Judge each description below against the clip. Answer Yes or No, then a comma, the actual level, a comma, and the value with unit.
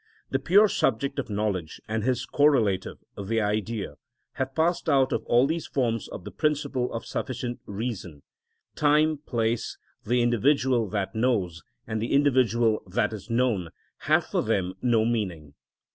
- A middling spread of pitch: Yes, average, 4.1 semitones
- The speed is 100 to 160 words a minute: Yes, average, 150 wpm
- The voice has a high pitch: No, low, 120 Hz